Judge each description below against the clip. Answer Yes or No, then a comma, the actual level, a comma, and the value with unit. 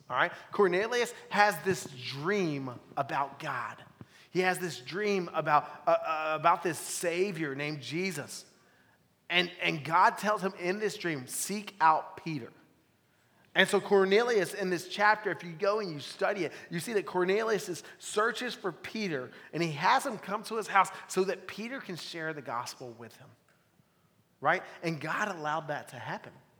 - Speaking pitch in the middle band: Yes, medium, 180 Hz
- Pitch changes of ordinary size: Yes, average, 4.4 semitones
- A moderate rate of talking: Yes, average, 170 wpm